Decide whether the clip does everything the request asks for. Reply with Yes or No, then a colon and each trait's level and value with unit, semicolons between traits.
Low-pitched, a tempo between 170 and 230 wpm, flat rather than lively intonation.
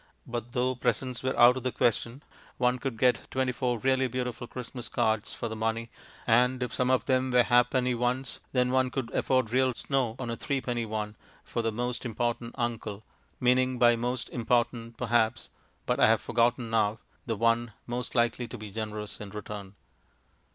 Yes: low, 120 Hz; average, 180 wpm; narrow, 1.8 semitones